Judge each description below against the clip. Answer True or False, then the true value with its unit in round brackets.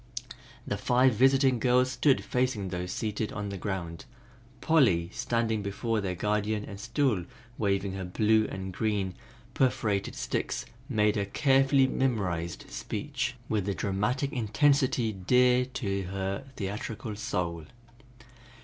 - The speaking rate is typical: False (125 wpm)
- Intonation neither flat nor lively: True (4.5 semitones)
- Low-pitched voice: True (105 Hz)